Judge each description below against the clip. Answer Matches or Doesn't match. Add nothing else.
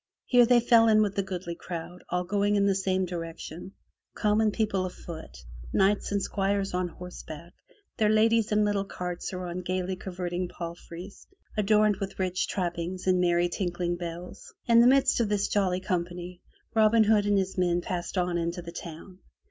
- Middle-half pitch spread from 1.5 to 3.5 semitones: Matches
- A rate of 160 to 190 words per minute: Matches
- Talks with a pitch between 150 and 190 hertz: Matches